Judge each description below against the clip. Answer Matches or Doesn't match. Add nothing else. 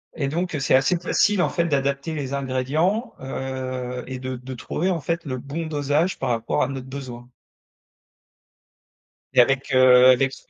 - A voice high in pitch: Doesn't match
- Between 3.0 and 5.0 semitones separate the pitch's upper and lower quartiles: Matches